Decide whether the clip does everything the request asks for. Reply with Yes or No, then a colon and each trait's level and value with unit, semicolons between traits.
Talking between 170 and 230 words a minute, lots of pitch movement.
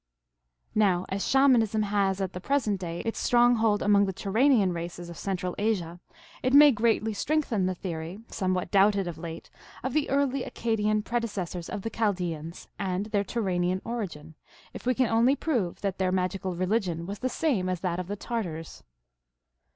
No: average, 175 wpm; average, 4.0 semitones